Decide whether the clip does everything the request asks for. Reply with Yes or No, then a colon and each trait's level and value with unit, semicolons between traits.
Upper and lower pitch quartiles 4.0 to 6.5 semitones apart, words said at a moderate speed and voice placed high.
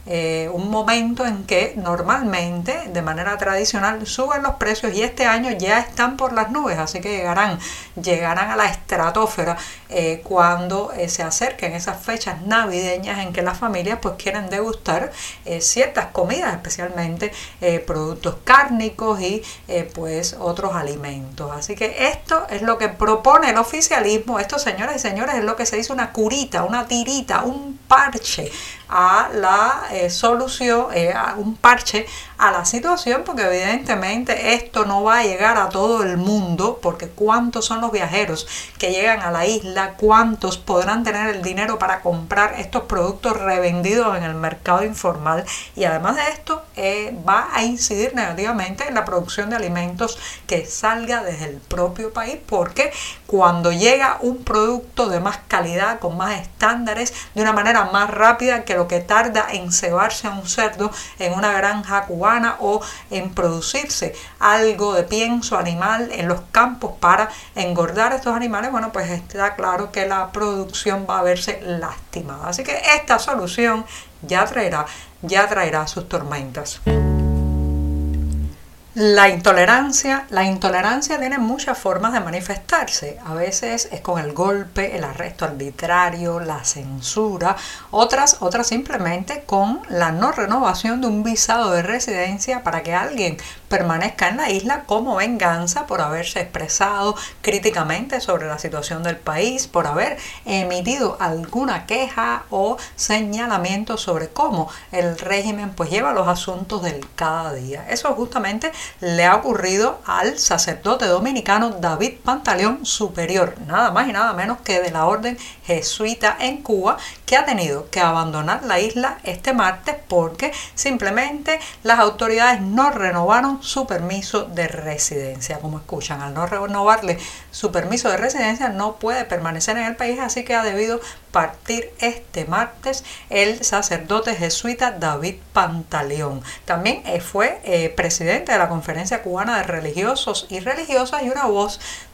Yes: average, 4.9 semitones; average, 150 wpm; high, 205 Hz